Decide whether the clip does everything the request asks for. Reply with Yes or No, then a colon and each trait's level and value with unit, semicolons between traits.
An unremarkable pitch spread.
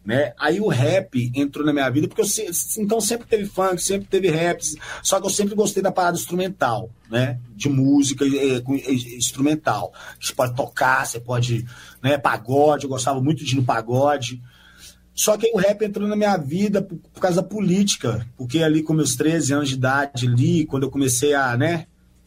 No: wide, 6.4 semitones